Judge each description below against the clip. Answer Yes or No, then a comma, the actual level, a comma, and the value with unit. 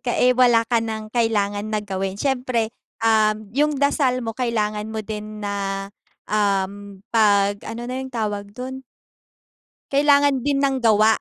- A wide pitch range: No, average, 3.4 semitones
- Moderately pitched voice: No, high, 220 Hz